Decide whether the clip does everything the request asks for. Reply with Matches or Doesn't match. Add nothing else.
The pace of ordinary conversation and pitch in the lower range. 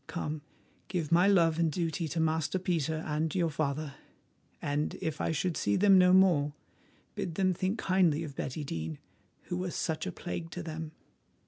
Doesn't match